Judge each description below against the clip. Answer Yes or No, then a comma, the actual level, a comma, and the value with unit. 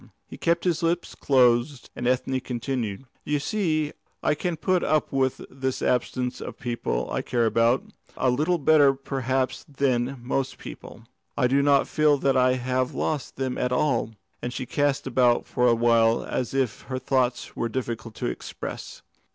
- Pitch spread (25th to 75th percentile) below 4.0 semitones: Yes, narrow, 2.6 semitones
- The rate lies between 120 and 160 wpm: No, average, 175 wpm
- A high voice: No, low, 130 Hz